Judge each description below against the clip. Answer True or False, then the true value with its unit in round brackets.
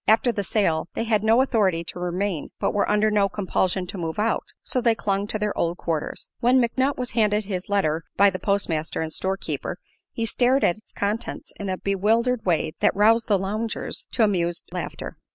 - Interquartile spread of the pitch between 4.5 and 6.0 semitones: False (3.5 semitones)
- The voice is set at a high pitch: True (205 Hz)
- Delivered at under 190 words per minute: False (200 wpm)